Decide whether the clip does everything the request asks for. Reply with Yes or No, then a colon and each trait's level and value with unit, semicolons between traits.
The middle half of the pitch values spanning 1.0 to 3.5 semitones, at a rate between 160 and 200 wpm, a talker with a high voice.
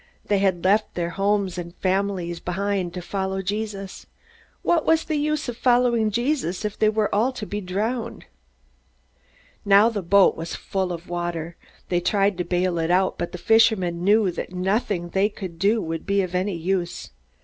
Yes: average, 3.2 semitones; average, 180 wpm; high, 195 Hz